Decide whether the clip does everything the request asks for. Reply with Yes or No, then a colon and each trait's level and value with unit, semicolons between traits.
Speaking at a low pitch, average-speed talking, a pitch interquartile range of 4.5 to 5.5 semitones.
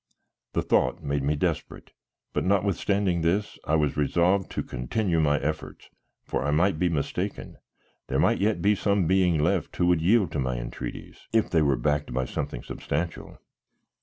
Yes: very low, 85 Hz; average, 170 wpm; average, 4.8 semitones